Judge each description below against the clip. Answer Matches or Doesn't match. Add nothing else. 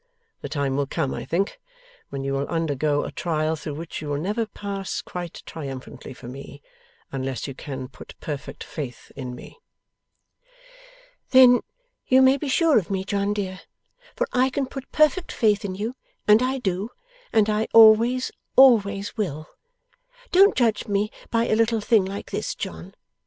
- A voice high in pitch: Matches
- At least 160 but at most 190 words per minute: Matches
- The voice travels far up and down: Matches